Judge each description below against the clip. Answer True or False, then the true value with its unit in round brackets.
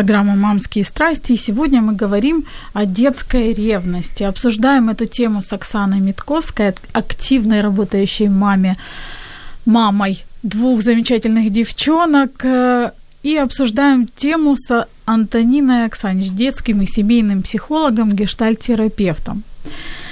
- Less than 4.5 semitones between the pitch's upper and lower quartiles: True (3.7 semitones)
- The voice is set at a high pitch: True (225 Hz)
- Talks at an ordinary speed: False (100 wpm)